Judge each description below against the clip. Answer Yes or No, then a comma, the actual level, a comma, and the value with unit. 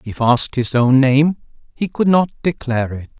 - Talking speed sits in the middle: Yes, average, 190 wpm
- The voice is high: No, low, 135 Hz